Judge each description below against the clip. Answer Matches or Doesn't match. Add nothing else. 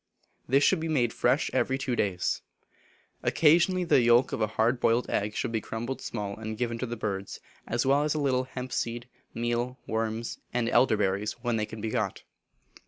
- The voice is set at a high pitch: Doesn't match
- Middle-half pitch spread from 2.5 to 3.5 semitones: Matches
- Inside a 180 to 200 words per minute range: Matches